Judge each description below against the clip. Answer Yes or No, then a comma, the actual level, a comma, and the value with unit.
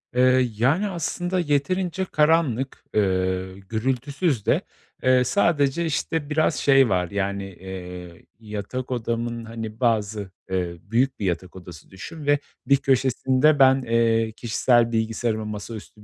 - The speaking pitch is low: Yes, low, 120 Hz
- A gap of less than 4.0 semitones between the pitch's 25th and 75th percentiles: No, average, 5.2 semitones